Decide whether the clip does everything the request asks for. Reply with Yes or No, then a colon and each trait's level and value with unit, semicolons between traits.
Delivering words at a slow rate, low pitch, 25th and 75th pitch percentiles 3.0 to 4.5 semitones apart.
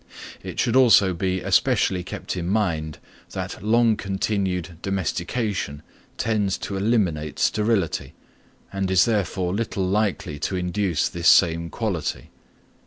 Yes: slow, 120 wpm; very low, 95 Hz; average, 3.4 semitones